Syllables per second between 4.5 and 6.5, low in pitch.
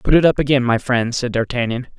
Yes: 6.0 syllables/s; low, 125 Hz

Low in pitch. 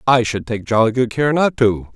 Yes: low, 120 Hz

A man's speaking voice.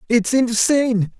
Yes: male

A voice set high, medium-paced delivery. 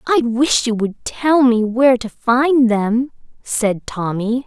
Yes: high, 240 Hz; average, 160 wpm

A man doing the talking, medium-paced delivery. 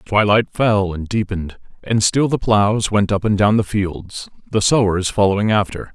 Yes: male; average, 180 wpm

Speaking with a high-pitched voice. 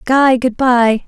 Yes: very high, 250 Hz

